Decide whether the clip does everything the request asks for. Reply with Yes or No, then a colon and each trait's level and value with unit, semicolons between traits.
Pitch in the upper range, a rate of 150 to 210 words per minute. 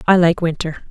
No: medium, 170 Hz; average, 200 wpm